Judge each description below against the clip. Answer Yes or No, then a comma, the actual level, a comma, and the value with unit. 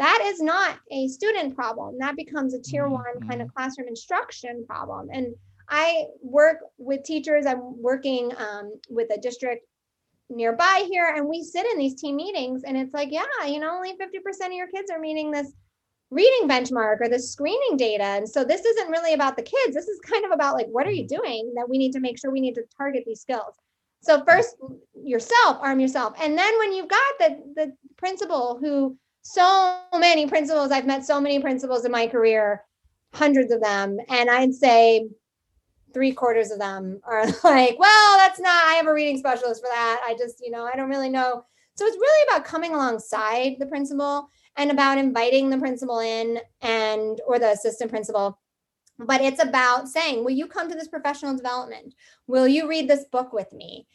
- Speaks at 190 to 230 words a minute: Yes, average, 200 wpm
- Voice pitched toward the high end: Yes, very high, 270 Hz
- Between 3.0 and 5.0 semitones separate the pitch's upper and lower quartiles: Yes, average, 4.7 semitones